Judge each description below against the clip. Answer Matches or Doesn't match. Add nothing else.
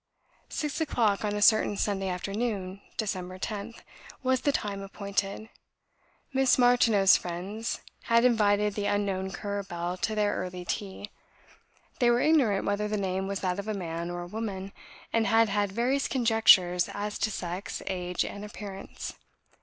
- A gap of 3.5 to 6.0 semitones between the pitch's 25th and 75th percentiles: Doesn't match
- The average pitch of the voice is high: Matches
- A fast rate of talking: Doesn't match